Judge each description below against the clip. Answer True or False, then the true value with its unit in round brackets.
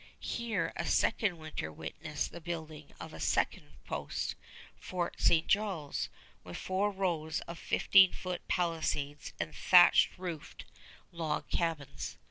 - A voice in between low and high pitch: True (165 Hz)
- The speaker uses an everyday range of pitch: True (3.2 semitones)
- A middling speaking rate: False (125 wpm)